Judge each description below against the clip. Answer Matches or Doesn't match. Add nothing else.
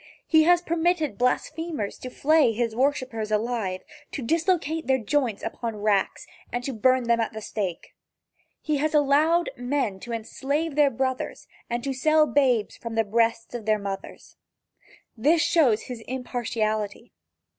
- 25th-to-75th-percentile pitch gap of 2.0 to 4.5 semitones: Doesn't match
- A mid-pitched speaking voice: Doesn't match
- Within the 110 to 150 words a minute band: Matches